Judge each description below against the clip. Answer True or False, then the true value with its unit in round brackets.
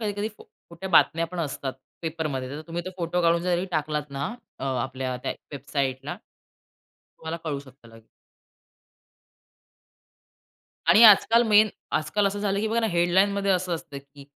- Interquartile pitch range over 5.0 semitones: True (5.5 semitones)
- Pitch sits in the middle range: True (165 Hz)